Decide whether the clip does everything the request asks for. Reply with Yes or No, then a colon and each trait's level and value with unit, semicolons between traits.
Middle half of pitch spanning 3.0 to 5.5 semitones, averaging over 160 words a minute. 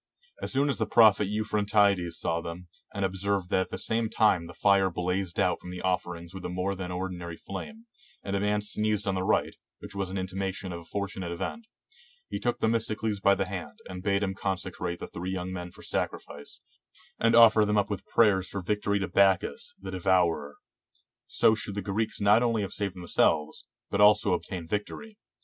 No: narrow, 2.4 semitones; average, 200 wpm